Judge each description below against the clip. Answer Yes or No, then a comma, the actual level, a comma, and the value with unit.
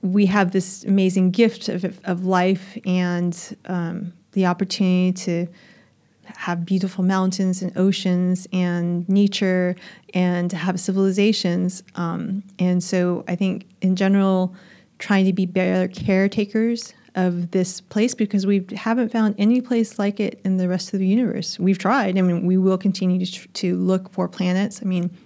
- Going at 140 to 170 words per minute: Yes, average, 160 wpm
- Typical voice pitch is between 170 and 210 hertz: Yes, high, 190 Hz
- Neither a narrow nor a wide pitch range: No, narrow, 1.7 semitones